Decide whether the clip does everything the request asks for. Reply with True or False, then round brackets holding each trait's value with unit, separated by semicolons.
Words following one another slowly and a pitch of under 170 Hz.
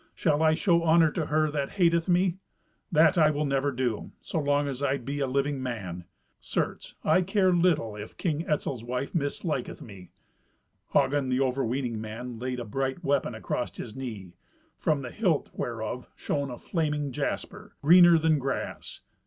False (170 wpm; 140 Hz)